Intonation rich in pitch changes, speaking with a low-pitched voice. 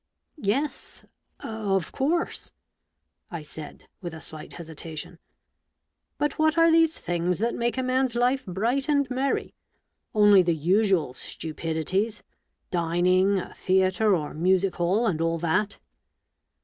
No: wide, 6.1 semitones; high, 190 Hz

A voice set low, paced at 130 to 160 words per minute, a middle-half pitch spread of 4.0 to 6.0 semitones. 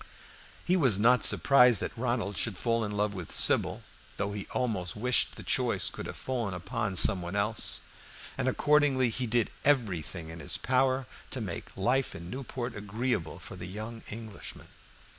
No: low, 110 Hz; average, 170 wpm; average, 4.4 semitones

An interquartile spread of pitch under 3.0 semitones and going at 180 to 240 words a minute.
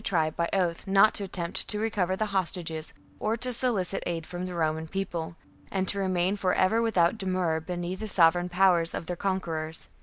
Yes: narrow, 2.6 semitones; average, 190 wpm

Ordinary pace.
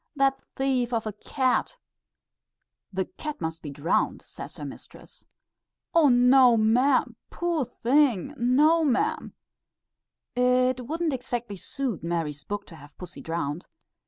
No: slow, 130 wpm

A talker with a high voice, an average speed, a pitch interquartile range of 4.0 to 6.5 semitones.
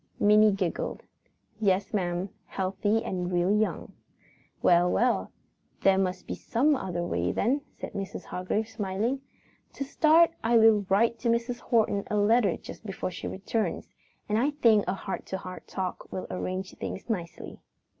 No: high, 205 Hz; average, 155 wpm; average, 3.5 semitones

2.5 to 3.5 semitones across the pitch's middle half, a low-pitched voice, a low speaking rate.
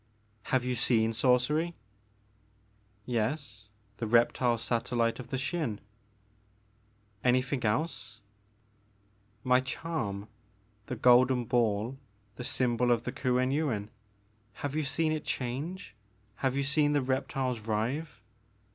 No: average, 3.9 semitones; low, 120 Hz; slow, 130 wpm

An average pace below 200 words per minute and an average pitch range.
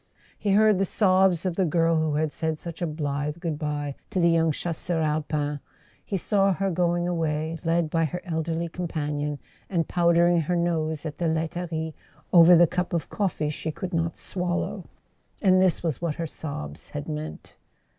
No: average, 175 wpm; narrow, 2.2 semitones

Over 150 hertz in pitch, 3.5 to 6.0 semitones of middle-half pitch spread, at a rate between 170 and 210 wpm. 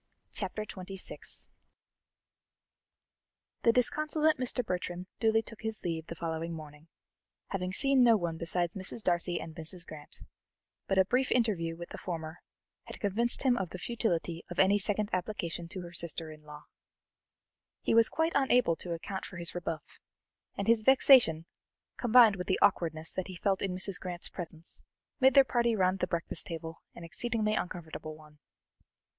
No: medium, 185 Hz; average, 5.0 semitones; average, 160 wpm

